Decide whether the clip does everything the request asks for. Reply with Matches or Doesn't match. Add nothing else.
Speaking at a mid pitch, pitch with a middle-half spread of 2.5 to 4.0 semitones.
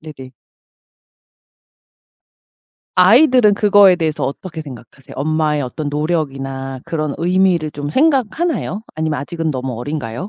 Doesn't match